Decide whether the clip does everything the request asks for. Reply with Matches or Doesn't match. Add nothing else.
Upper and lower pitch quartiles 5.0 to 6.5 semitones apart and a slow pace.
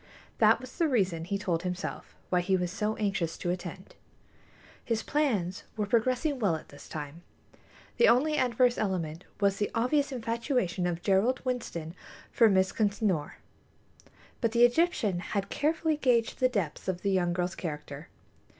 Doesn't match